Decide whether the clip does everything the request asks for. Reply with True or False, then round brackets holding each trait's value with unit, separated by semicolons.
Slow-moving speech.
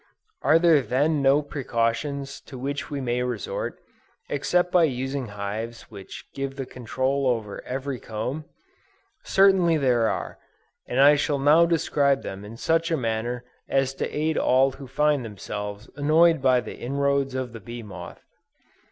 False (155 wpm)